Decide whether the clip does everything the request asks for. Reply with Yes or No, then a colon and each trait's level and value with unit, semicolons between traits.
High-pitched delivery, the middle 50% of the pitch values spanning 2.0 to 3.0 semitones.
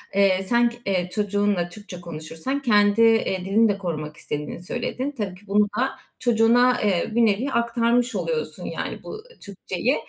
No: high, 210 Hz; average, 4.1 semitones